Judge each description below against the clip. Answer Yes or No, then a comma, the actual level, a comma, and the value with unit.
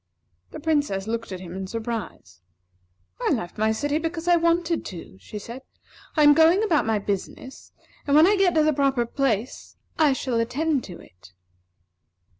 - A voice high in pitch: Yes, very high, 265 Hz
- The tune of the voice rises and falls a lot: Yes, wide, 6.7 semitones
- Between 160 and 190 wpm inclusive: Yes, average, 175 wpm